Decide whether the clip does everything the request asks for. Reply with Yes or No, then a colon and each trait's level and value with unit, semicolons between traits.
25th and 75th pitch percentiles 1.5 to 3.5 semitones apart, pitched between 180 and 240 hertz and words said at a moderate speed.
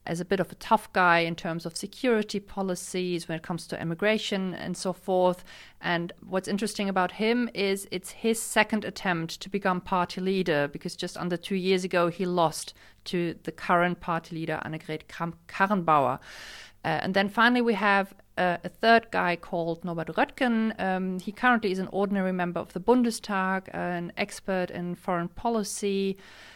Yes: narrow, 2.6 semitones; medium, 185 Hz; average, 175 wpm